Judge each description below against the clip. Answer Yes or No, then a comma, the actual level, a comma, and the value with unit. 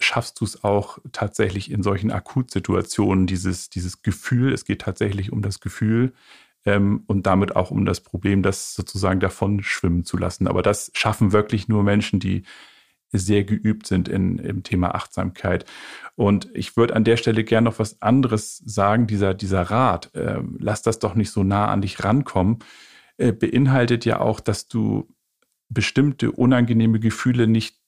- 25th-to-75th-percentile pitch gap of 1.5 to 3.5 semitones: Yes, narrow, 2.4 semitones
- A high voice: No, low, 105 Hz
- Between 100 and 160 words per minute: No, average, 170 wpm